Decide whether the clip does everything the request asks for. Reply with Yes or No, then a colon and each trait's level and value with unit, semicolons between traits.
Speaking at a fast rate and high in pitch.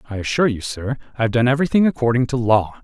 No: fast, 235 wpm; low, 125 Hz